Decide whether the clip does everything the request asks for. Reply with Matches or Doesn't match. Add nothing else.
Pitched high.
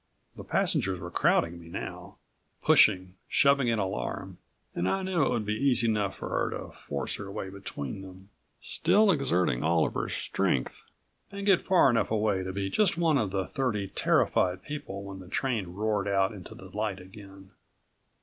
Doesn't match